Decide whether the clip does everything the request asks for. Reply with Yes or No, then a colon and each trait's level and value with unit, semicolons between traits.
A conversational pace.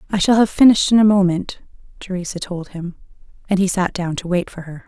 No: fast, 220 wpm